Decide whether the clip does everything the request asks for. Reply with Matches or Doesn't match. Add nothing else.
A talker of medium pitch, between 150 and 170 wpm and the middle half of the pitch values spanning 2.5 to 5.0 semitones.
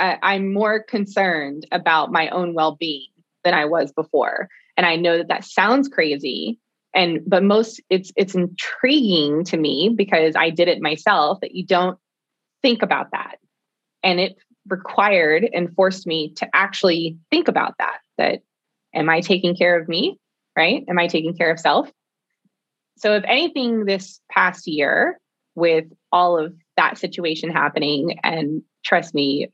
Matches